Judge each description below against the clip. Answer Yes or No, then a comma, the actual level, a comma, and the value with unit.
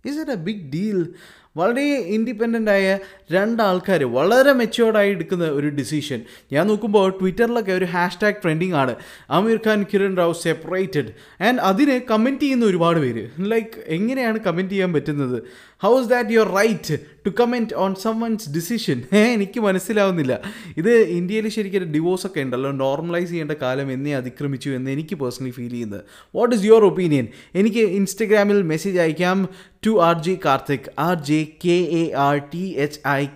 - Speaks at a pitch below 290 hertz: Yes, medium, 185 Hz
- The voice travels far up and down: Yes, wide, 6.4 semitones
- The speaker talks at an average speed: No, fast, 150 wpm